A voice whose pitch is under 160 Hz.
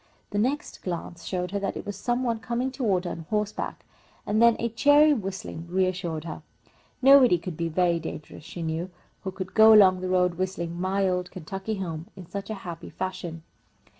No: medium, 185 Hz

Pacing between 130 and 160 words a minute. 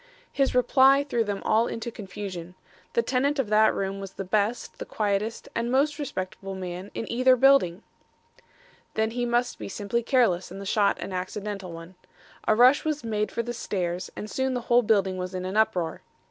No: average, 190 wpm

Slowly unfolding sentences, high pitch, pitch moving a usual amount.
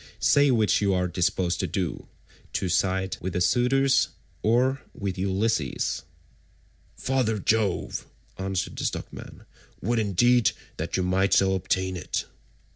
No: slow, 125 wpm; very low, 95 Hz; average, 3.8 semitones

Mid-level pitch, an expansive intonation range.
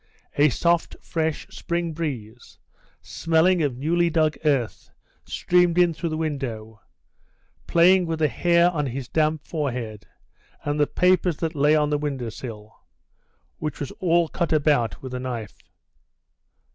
No: medium, 155 Hz; average, 4.4 semitones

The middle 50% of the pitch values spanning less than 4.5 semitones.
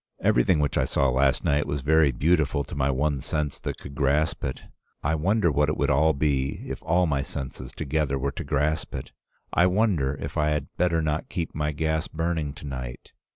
Yes: narrow, 2.4 semitones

